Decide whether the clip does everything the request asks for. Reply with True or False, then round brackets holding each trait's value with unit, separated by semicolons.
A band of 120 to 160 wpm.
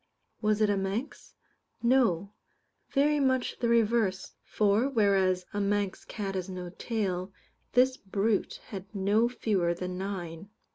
True (135 wpm)